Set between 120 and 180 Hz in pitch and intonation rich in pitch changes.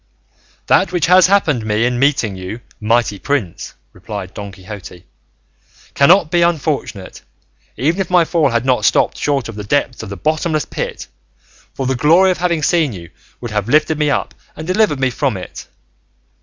Yes: low, 135 Hz; wide, 7.0 semitones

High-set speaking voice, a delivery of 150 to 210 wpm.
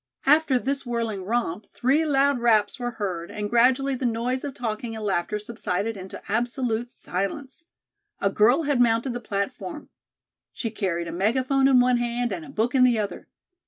Yes: high, 240 Hz; average, 175 wpm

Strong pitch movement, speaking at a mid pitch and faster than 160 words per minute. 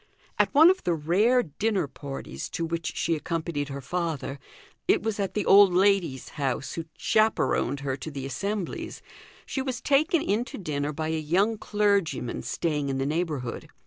Yes: wide, 6.1 semitones; medium, 170 Hz; average, 175 wpm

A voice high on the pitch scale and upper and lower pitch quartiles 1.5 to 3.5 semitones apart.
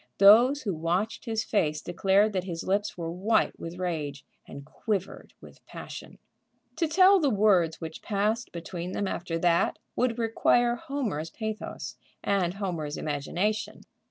No: high, 195 Hz; average, 4.8 semitones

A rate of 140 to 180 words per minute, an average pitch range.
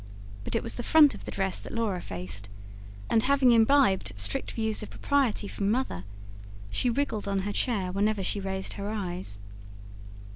Yes: average, 175 wpm; average, 3.8 semitones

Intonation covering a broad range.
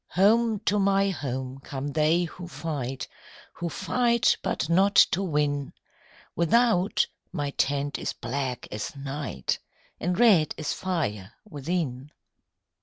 Yes: wide, 5.7 semitones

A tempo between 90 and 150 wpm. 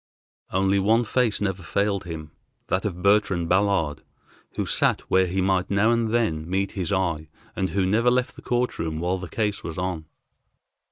No: average, 180 wpm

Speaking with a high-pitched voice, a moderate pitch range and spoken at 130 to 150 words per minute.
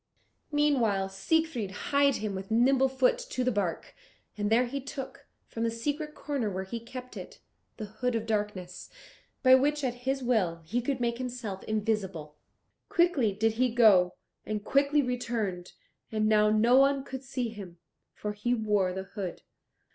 No: high, 230 Hz; average, 4.2 semitones; average, 165 wpm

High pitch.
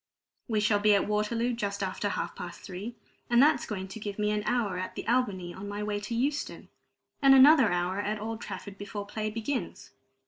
Yes: high, 210 Hz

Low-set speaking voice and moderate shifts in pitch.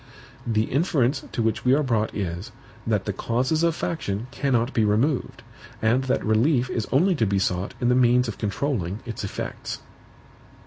Yes: low, 120 Hz; average, 4.0 semitones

